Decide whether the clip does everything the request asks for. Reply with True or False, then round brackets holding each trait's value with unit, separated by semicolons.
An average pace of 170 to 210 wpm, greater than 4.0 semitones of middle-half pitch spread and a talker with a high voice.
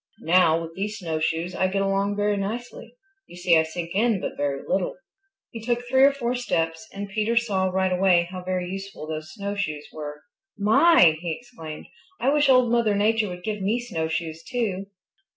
True (185 wpm; 5.2 semitones; 195 Hz)